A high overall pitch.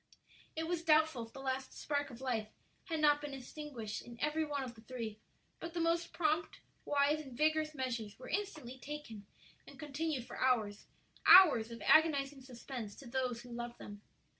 Yes: very high, 270 Hz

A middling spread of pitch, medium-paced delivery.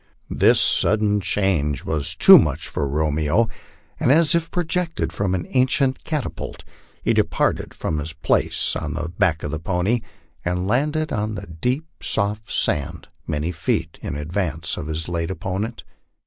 No: wide, 6.7 semitones; average, 155 wpm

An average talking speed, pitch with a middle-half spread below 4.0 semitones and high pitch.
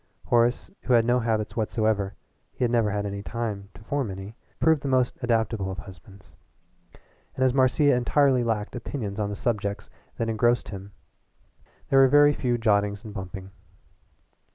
No: average, 160 wpm; average, 3.4 semitones; low, 110 Hz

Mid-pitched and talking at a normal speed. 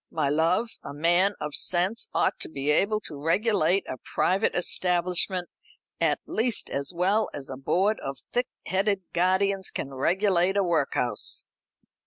Yes: medium, 180 Hz; average, 150 wpm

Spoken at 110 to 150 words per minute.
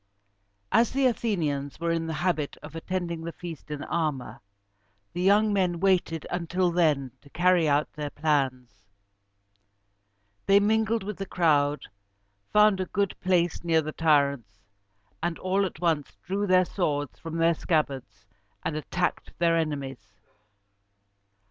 Yes: average, 140 wpm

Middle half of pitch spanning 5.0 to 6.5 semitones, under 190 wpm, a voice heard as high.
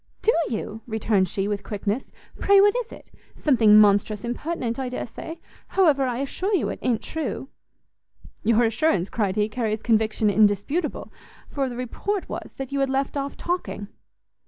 Yes: average, 5.3 semitones; average, 165 wpm; high, 240 Hz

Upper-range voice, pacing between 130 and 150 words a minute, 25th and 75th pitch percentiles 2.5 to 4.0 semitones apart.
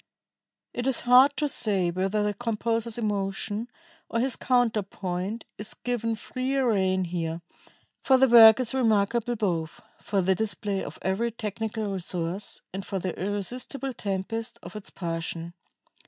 Yes: high, 210 Hz; average, 140 wpm; average, 3.7 semitones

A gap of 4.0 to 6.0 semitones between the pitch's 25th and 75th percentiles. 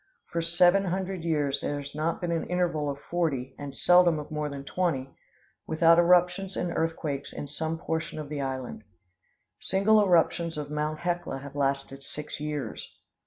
No: average, 3.5 semitones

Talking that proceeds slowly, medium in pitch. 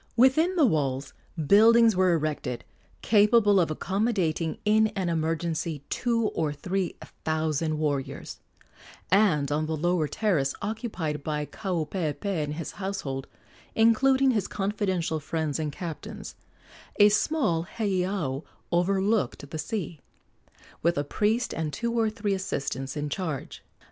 Yes: slow, 125 wpm; medium, 175 Hz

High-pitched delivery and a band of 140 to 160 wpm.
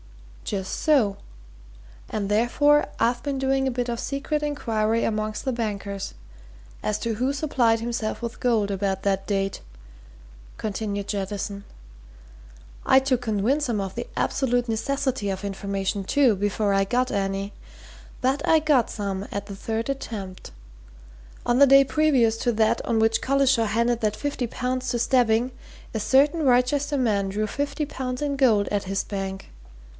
Yes: high, 230 Hz; average, 155 wpm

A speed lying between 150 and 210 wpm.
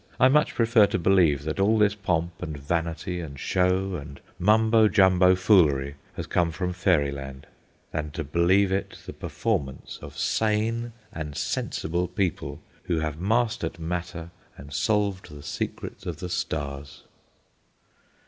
No: average, 140 wpm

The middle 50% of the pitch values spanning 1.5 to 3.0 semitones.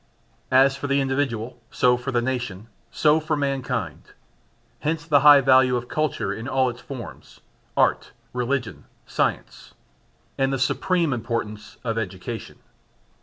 Yes: average, 2.7 semitones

